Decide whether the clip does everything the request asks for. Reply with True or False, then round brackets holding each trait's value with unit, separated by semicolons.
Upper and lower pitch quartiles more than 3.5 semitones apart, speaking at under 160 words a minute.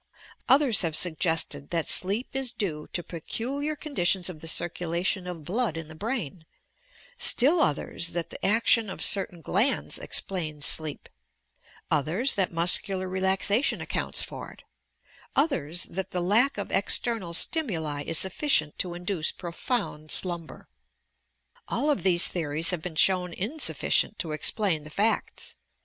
True (5.1 semitones; 140 wpm)